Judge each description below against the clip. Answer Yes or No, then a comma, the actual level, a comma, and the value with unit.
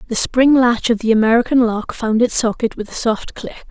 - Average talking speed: No, fast, 225 wpm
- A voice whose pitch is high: Yes, high, 230 Hz